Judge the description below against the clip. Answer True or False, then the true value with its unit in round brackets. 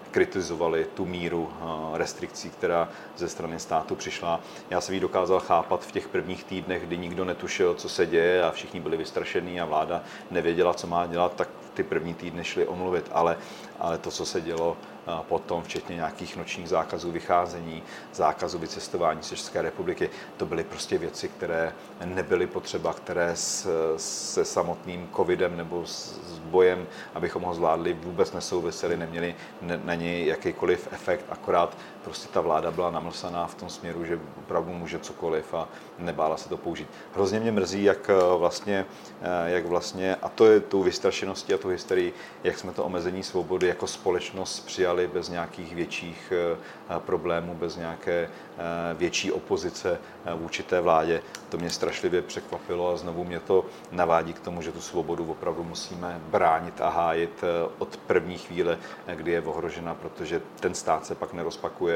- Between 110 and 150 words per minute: False (160 wpm)